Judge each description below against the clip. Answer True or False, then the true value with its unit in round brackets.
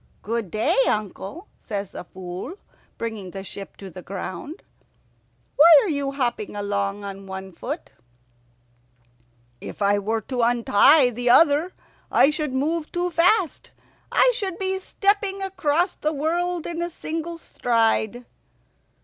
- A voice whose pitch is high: True (265 Hz)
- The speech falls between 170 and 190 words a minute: False (135 wpm)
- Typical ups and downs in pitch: False (8.7 semitones)